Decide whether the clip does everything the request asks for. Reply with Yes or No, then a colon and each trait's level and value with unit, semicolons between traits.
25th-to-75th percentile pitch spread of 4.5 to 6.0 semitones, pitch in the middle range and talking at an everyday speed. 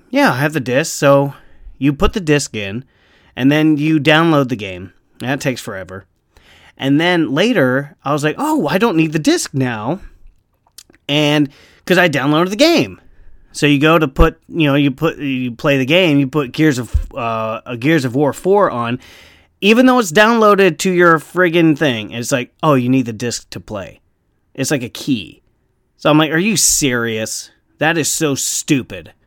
Yes: average, 5.1 semitones; medium, 145 Hz; average, 190 wpm